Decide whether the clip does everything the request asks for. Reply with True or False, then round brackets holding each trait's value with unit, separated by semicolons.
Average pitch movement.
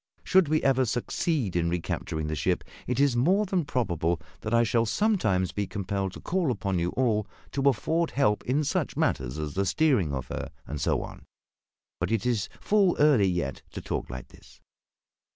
False (8.0 semitones)